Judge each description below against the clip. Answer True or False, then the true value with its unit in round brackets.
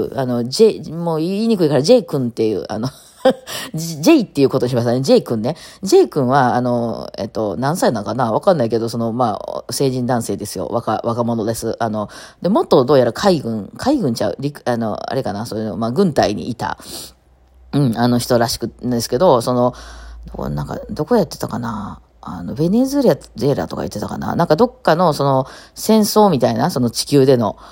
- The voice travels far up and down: True (5.8 semitones)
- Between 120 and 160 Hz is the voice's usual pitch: True (125 Hz)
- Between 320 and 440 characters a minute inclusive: True (365 characters per minute)